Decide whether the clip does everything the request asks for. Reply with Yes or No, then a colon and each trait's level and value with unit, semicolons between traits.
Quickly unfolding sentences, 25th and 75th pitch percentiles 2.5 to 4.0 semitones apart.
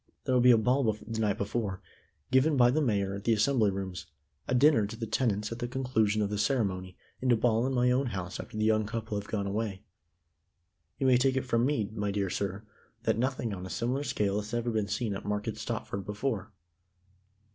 Yes: fast, 215 wpm; average, 3.6 semitones